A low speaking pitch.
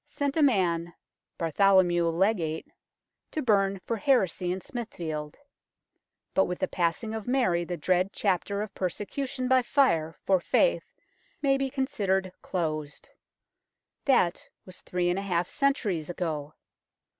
No: high, 190 Hz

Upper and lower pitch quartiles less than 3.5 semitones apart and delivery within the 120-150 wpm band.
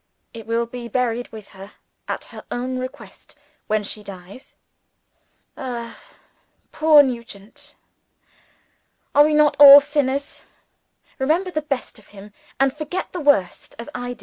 No: average, 4.3 semitones; average, 140 wpm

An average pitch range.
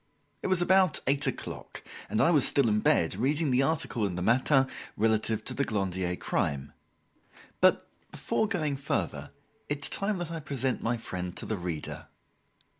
No: wide, 6.8 semitones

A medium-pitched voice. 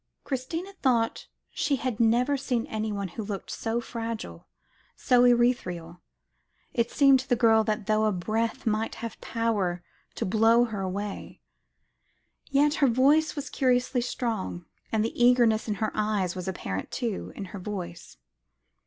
No: high, 225 Hz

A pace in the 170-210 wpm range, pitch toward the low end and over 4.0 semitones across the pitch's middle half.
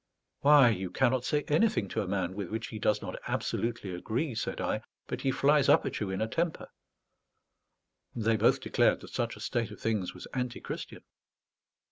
Yes: average, 185 wpm; low, 115 Hz; average, 4.7 semitones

